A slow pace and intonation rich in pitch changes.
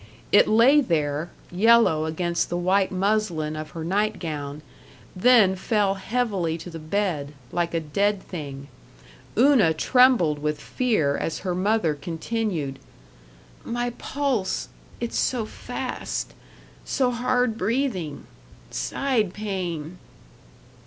Yes: slow, 110 wpm; wide, 6.0 semitones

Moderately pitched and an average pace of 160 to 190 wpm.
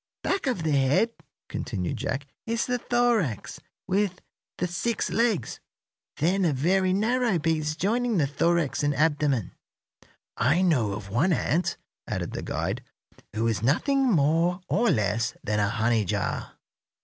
No: medium, 165 Hz; average, 145 wpm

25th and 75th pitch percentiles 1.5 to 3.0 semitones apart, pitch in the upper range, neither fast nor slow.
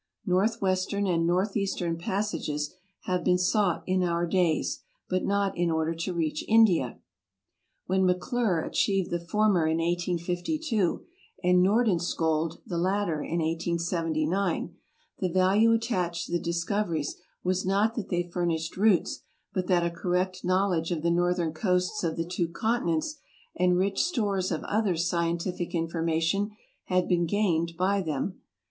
No: narrow, 2.5 semitones; medium, 180 Hz; average, 145 wpm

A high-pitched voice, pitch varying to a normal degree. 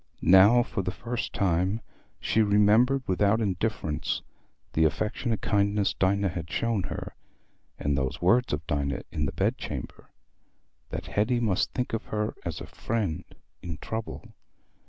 No: low, 100 Hz; average, 5.0 semitones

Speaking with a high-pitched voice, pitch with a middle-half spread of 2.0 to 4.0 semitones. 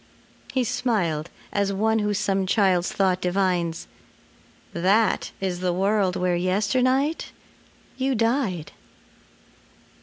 Yes: high, 195 Hz; average, 3.5 semitones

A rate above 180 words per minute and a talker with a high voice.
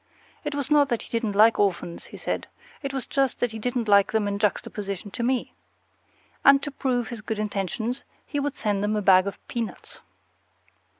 Yes: average, 195 wpm; high, 225 Hz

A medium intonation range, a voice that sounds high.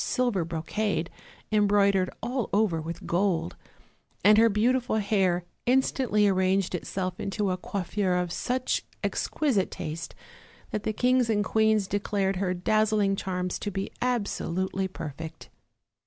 Yes: average, 3.0 semitones; high, 200 Hz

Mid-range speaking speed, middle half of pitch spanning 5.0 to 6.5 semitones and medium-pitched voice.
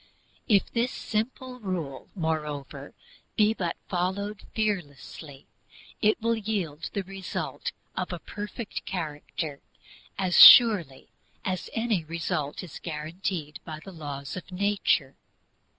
No: slow, 120 wpm; wide, 5.5 semitones; medium, 180 Hz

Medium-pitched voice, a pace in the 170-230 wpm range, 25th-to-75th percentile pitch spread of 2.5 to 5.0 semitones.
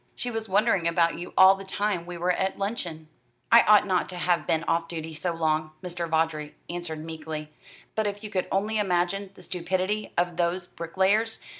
Yes: medium, 175 Hz; average, 190 wpm; average, 3.0 semitones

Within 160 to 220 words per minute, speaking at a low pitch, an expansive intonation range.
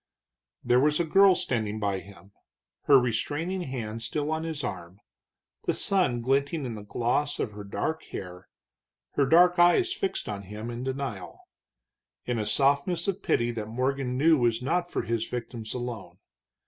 Yes: average, 165 wpm; low, 125 Hz; wide, 5.9 semitones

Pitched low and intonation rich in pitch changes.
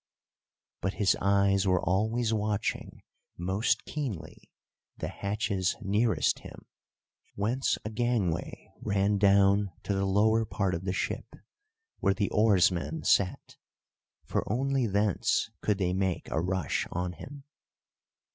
No: low, 100 Hz; narrow, 2.6 semitones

